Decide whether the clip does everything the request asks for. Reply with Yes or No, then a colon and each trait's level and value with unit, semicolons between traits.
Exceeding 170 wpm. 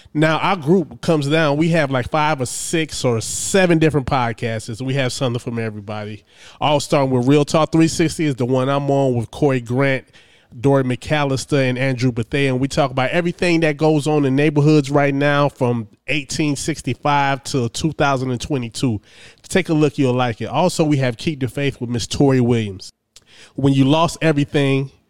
Yes: average, 180 wpm